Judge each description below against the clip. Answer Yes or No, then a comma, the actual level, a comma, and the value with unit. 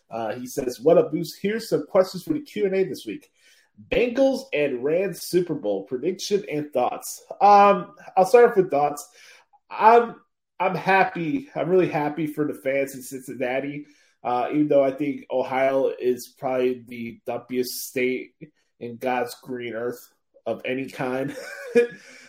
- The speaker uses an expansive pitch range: Yes, wide, 7.0 semitones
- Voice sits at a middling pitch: Yes, medium, 145 Hz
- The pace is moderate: Yes, average, 160 wpm